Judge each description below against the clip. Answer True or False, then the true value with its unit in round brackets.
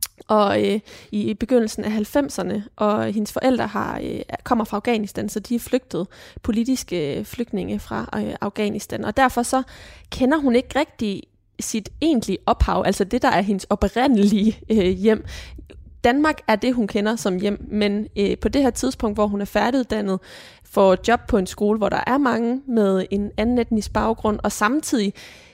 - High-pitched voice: True (215 Hz)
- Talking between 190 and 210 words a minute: False (175 wpm)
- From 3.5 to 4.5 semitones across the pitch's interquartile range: False (3.1 semitones)